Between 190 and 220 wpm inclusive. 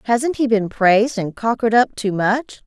Yes: fast, 205 wpm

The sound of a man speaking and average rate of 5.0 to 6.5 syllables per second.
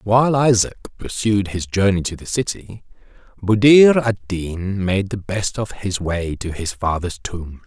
No: male; 4.2 syllables/s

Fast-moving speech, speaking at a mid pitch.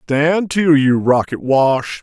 No: average, 150 wpm; medium, 145 Hz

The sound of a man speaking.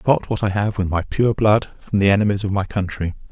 Yes: male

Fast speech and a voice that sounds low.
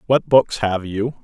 No: average, 195 wpm; low, 110 Hz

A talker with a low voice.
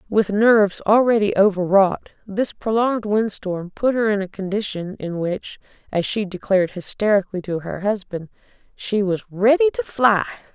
No: high, 205 Hz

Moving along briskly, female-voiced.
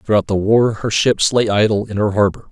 No: fast, 240 wpm; male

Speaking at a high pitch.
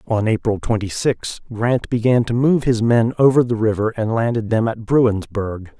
No: low, 115 Hz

